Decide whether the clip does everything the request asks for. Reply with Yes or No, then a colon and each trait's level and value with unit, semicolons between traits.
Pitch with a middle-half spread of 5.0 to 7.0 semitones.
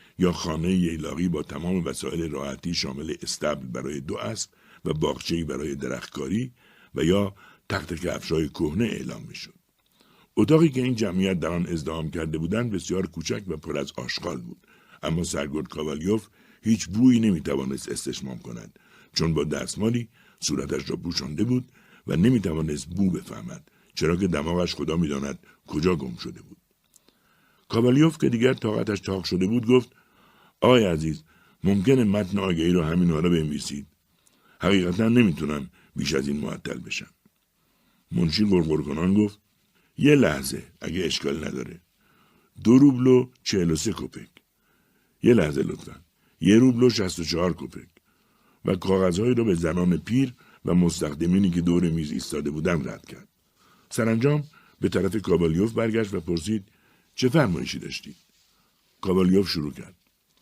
Yes: wide, 5.4 semitones